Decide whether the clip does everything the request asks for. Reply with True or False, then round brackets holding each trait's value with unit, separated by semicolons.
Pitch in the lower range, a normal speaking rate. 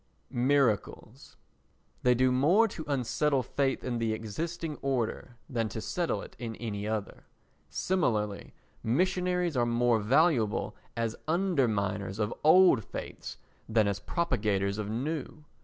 False (120 Hz; 125 wpm)